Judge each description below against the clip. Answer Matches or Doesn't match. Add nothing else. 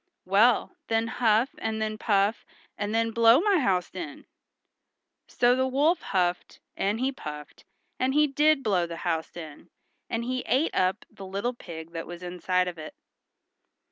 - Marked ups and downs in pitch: Matches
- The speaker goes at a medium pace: Matches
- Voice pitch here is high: Matches